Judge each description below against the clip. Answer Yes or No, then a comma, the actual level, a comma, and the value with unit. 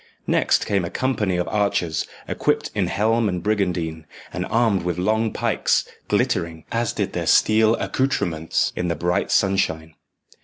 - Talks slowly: No, average, 150 wpm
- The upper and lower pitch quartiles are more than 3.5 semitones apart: Yes, average, 4.2 semitones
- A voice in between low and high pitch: No, very low, 95 Hz